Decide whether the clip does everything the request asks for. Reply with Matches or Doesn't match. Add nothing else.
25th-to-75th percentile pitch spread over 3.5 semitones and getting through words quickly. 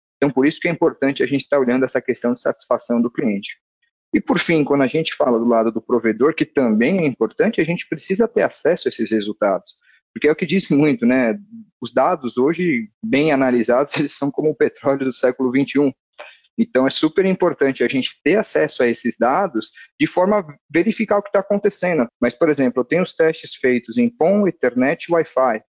Matches